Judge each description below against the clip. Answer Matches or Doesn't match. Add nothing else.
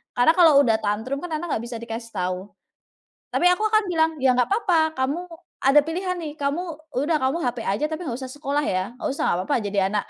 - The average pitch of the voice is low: Doesn't match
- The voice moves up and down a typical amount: Doesn't match